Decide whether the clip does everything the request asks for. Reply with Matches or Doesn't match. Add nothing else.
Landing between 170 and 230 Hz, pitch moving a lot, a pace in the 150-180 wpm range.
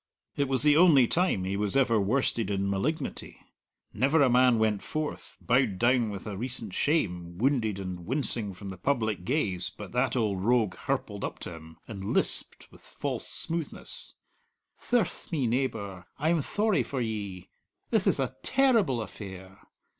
Doesn't match